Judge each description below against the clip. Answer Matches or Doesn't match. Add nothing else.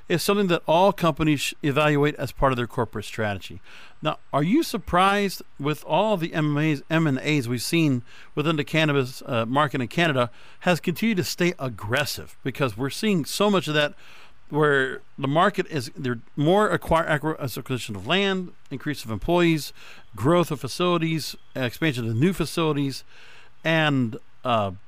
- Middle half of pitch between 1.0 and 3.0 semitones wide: Doesn't match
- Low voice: Doesn't match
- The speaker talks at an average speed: Matches